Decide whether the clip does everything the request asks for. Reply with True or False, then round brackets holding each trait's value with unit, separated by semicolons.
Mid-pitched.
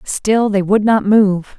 False (205 Hz)